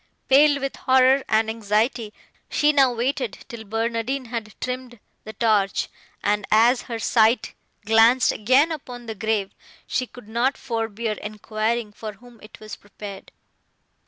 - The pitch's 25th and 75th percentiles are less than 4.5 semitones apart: Yes, average, 2.9 semitones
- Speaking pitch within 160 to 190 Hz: No, high, 230 Hz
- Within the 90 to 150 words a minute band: Yes, average, 140 wpm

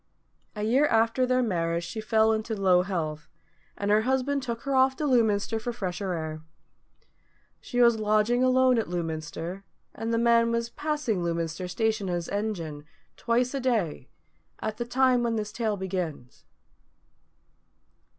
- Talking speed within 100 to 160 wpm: Yes, average, 155 wpm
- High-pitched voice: Yes, high, 220 Hz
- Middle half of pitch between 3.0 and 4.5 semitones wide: No, average, 5.1 semitones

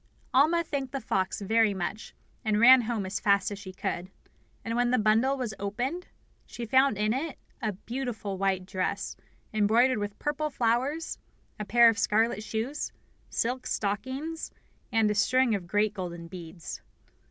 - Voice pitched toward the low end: No, high, 220 Hz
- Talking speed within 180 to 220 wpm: No, average, 160 wpm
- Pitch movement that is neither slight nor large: Yes, average, 4.4 semitones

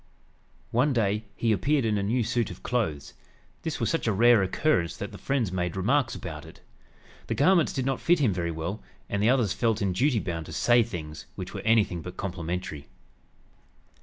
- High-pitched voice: No, low, 105 Hz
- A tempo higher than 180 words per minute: Yes, average, 195 wpm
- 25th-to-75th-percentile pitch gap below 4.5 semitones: No, wide, 5.5 semitones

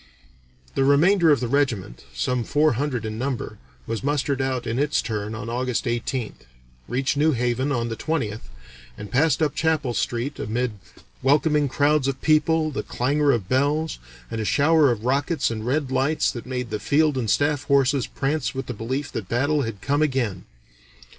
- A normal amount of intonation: Yes, average, 3.8 semitones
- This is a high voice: No, low, 130 Hz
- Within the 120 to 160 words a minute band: No, average, 180 wpm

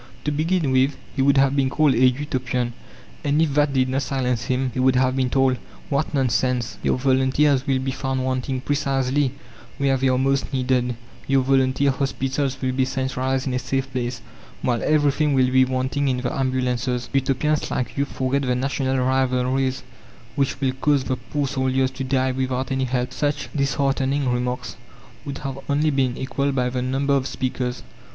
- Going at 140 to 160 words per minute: No, average, 180 wpm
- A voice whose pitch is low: Yes, low, 130 Hz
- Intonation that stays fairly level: Yes, narrow, 1.3 semitones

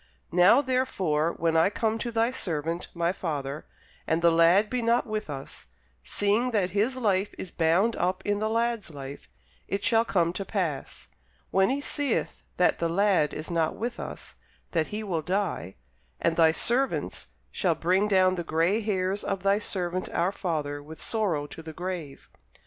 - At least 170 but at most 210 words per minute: Yes, average, 175 wpm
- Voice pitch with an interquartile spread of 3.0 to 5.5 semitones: Yes, average, 4.6 semitones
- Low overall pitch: No, medium, 185 Hz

